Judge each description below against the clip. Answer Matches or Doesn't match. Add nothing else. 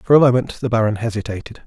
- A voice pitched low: Matches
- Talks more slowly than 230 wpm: Matches